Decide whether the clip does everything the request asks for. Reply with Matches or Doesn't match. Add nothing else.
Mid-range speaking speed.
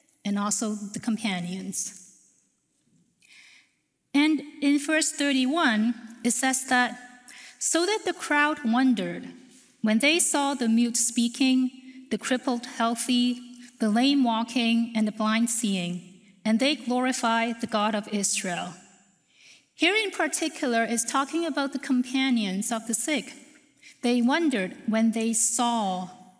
Doesn't match